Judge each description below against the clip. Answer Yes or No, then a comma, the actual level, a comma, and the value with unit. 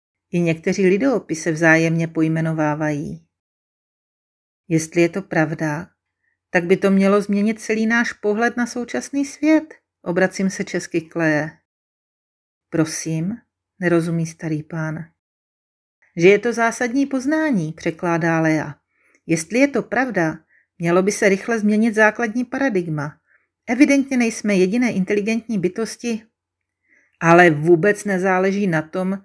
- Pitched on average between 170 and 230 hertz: Yes, medium, 185 Hz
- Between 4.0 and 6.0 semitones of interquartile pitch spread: Yes, wide, 5.5 semitones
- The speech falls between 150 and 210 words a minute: No, slow, 115 wpm